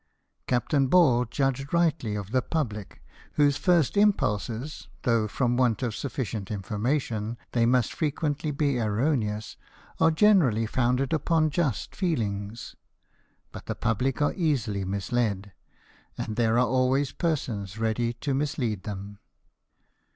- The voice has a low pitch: Yes, low, 125 Hz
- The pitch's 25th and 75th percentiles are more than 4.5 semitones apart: Yes, average, 5.1 semitones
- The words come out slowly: Yes, slow, 130 wpm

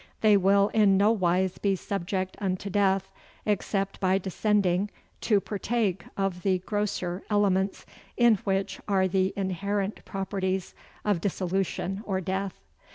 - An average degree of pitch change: No, narrow, 1.3 semitones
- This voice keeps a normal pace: No, slow, 130 wpm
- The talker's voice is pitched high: Yes, high, 195 Hz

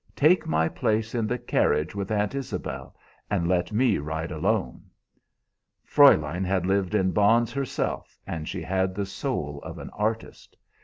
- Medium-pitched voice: No, low, 100 Hz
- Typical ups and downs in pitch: Yes, average, 4.3 semitones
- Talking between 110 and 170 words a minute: Yes, average, 155 wpm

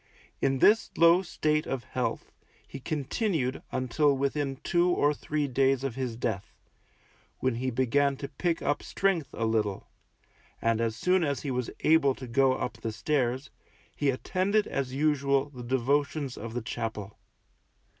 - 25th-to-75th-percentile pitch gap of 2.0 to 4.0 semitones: Yes, average, 3.4 semitones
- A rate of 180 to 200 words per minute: No, average, 155 wpm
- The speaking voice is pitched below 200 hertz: Yes, low, 135 Hz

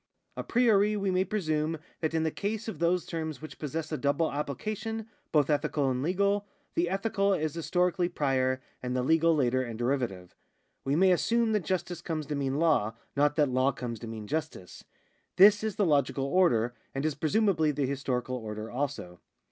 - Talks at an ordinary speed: Yes, average, 185 wpm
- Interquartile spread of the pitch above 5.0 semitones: Yes, wide, 5.5 semitones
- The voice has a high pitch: No, medium, 155 Hz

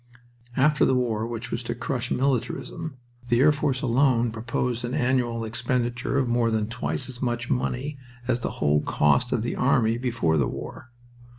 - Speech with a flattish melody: Yes, narrow, 1.9 semitones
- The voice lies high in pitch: No, low, 120 Hz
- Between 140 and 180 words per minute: Yes, average, 175 wpm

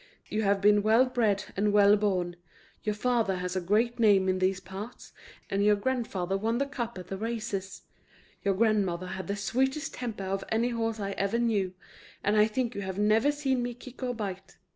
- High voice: Yes, high, 210 Hz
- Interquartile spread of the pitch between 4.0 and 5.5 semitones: No, average, 3.4 semitones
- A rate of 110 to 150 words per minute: No, average, 200 wpm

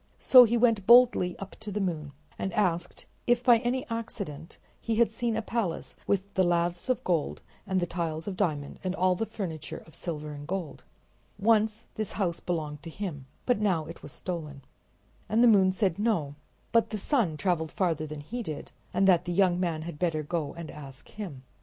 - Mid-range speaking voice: Yes, medium, 180 Hz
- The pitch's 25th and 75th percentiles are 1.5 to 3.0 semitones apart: No, average, 5.0 semitones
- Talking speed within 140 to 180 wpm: No, fast, 205 wpm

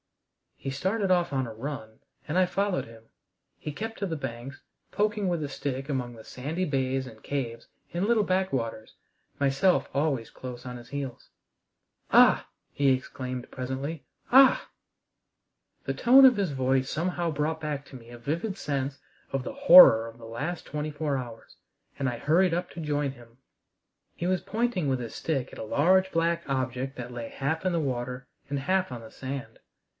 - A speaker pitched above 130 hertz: Yes, medium, 140 Hz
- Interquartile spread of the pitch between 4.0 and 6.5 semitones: Yes, wide, 5.5 semitones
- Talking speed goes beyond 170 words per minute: Yes, average, 180 wpm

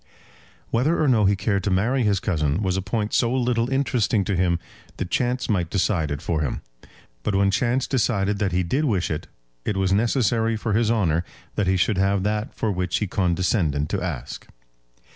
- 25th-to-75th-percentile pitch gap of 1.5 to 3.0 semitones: No, average, 4.2 semitones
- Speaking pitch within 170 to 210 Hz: No, low, 100 Hz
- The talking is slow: No, average, 200 wpm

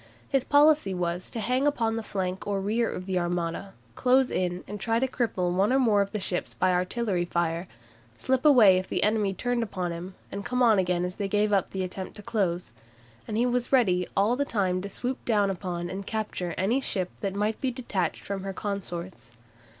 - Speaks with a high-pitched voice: Yes, high, 200 Hz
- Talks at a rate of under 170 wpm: No, fast, 205 wpm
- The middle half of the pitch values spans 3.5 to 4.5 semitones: Yes, average, 4.2 semitones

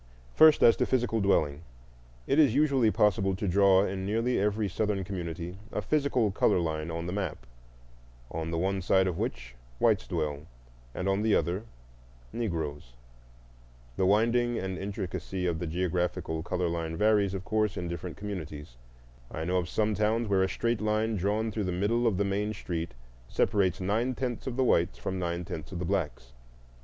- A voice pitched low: Yes, very low, 95 Hz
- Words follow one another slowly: No, average, 175 wpm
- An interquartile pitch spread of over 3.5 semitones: Yes, average, 3.9 semitones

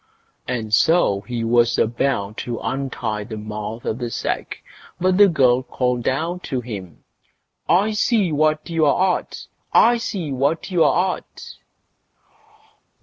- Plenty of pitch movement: Yes, wide, 6.9 semitones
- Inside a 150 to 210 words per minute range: No, slow, 135 wpm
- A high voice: No, low, 130 Hz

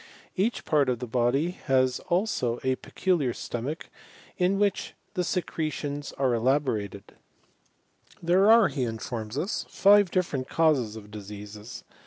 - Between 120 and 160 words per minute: Yes, slow, 135 wpm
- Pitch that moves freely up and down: Yes, wide, 7.1 semitones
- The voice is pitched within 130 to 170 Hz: Yes, low, 135 Hz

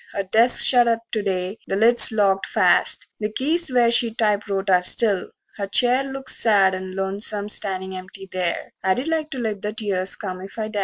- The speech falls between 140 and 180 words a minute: No, average, 200 wpm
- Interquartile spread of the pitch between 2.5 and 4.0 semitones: Yes, average, 3.4 semitones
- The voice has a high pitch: Yes, high, 210 Hz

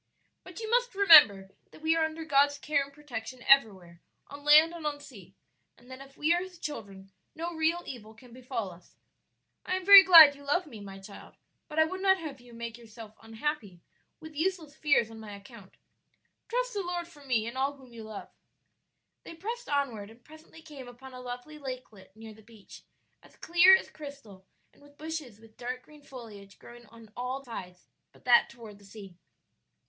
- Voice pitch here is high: Yes, very high, 265 Hz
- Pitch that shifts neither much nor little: No, wide, 6.1 semitones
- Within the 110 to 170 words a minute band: No, average, 195 wpm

